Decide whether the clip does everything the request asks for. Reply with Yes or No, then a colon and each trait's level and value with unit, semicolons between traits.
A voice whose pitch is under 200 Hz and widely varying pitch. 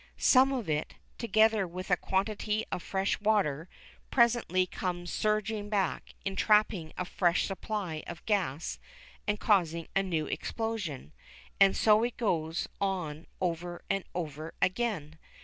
No: high, 190 Hz; average, 4.1 semitones